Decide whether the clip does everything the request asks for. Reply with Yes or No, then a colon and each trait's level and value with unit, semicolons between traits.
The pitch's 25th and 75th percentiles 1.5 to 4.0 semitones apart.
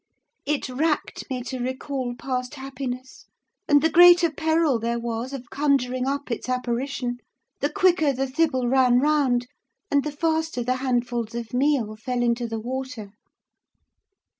Yes: average, 3.0 semitones